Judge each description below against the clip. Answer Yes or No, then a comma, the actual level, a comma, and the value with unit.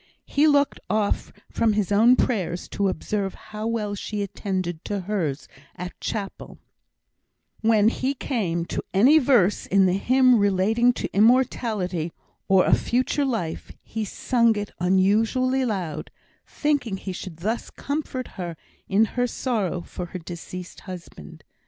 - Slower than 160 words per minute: Yes, average, 140 wpm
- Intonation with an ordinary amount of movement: Yes, average, 4.6 semitones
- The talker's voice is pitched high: Yes, high, 205 Hz